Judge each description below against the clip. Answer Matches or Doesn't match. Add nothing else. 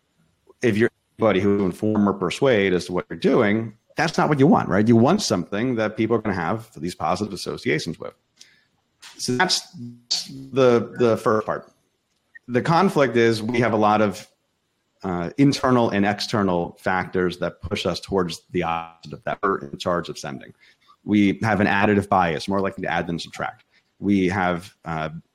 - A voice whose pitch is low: Matches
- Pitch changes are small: Doesn't match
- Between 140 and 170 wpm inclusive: Doesn't match